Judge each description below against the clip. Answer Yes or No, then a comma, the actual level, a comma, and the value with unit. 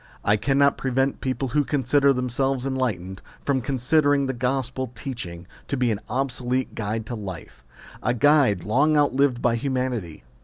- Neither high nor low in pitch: No, low, 130 Hz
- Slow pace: No, average, 155 wpm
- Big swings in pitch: No, average, 3.0 semitones